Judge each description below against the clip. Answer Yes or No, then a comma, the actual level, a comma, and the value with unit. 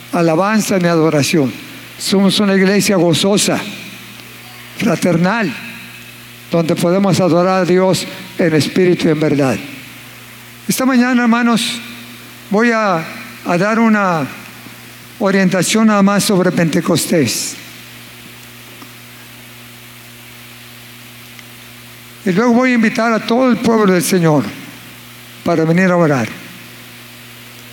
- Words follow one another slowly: Yes, slow, 100 wpm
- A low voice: No, medium, 170 Hz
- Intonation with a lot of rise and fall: Yes, wide, 8.4 semitones